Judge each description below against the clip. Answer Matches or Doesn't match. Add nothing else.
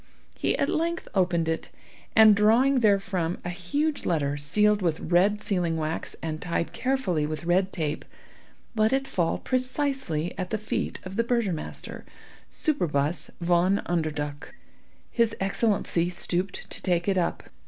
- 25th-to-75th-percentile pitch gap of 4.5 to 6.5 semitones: Matches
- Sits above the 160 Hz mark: Matches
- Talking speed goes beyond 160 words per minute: Doesn't match